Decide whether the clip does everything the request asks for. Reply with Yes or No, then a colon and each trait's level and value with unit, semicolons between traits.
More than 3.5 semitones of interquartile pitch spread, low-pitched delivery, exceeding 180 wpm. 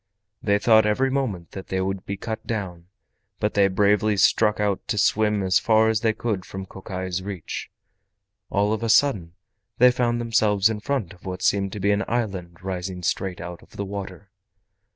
No: average, 2.7 semitones; low, 100 Hz; average, 190 wpm